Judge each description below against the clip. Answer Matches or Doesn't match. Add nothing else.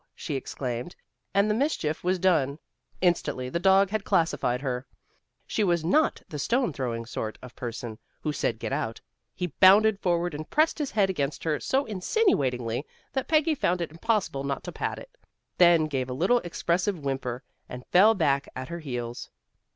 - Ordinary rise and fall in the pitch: Doesn't match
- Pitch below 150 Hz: Doesn't match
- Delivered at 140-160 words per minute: Doesn't match